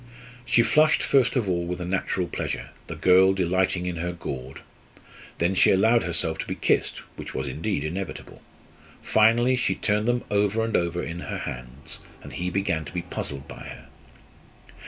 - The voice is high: No, very low, 90 Hz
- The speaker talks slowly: No, average, 175 wpm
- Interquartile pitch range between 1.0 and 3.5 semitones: No, average, 4.1 semitones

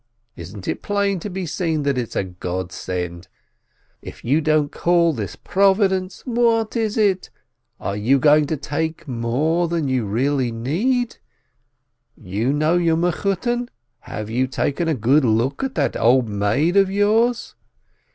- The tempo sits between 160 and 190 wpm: No, average, 145 wpm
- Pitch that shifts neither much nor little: No, wide, 8.4 semitones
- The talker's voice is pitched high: No, medium, 150 Hz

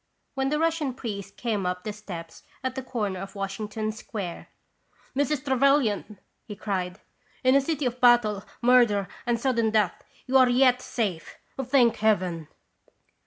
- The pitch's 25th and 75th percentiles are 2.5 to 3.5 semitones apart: No, average, 4.5 semitones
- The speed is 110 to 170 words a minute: Yes, average, 165 wpm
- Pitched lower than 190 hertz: No, high, 225 Hz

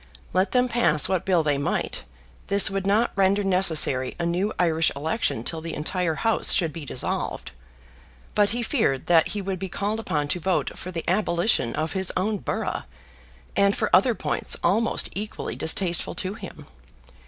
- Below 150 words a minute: No, average, 175 wpm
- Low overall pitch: No, medium, 185 Hz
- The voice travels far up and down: No, average, 3.9 semitones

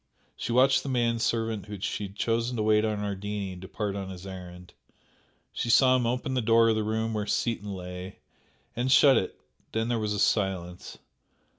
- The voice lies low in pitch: Yes, low, 110 Hz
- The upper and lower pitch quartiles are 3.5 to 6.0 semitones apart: No, average, 3.1 semitones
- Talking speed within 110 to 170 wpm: No, average, 190 wpm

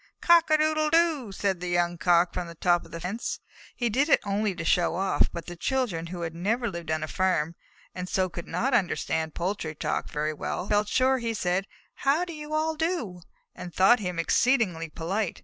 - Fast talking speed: Yes, fast, 220 wpm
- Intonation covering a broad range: Yes, wide, 6.8 semitones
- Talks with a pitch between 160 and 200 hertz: Yes, high, 190 Hz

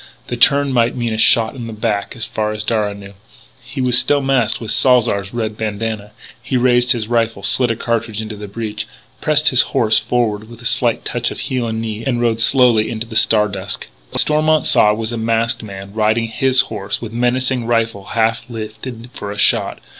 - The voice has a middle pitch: No, low, 115 Hz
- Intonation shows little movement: Yes, narrow, 2.2 semitones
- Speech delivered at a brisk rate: Yes, fast, 215 wpm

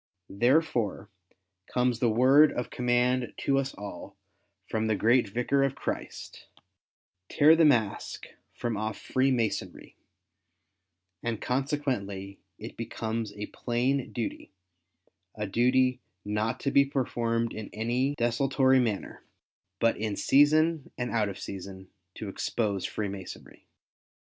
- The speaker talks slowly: Yes, slow, 125 wpm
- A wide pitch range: No, average, 3.5 semitones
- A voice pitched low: Yes, low, 120 Hz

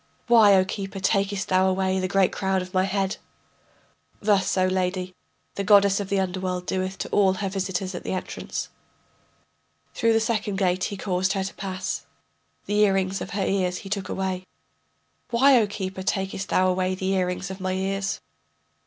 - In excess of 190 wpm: No, average, 180 wpm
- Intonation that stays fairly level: Yes, narrow, 1.1 semitones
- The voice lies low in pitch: No, high, 190 Hz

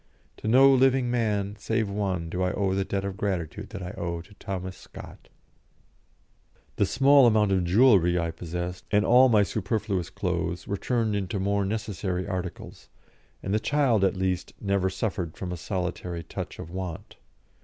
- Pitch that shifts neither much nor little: Yes, average, 3.1 semitones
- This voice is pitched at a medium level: No, very low, 95 Hz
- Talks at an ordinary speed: Yes, average, 165 wpm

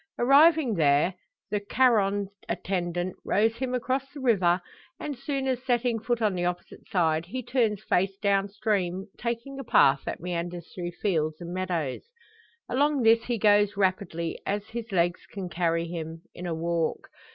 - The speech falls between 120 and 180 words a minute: Yes, average, 165 wpm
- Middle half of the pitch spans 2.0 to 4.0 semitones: No, wide, 5.4 semitones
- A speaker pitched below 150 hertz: No, high, 200 Hz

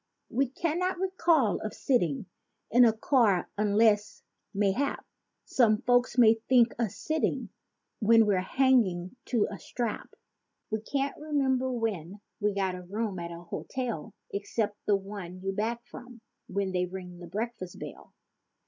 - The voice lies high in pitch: Yes, high, 220 Hz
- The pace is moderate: Yes, average, 145 wpm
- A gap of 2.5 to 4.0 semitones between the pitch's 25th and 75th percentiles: No, average, 4.4 semitones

